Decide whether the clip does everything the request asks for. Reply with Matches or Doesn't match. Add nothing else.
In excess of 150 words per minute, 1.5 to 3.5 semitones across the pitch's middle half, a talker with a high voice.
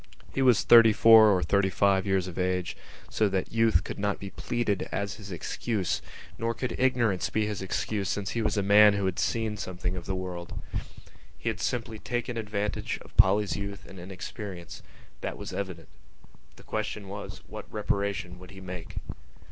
Doesn't match